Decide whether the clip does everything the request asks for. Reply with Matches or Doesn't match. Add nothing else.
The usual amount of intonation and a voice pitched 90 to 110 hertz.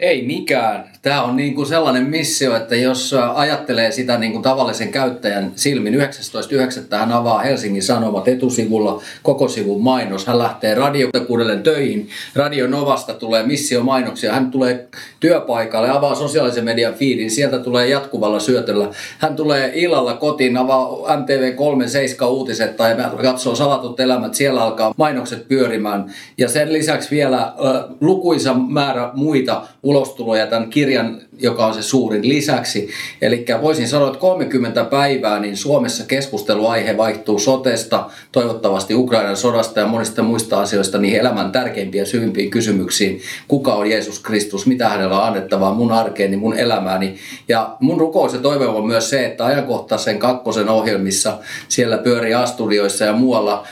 Doesn't match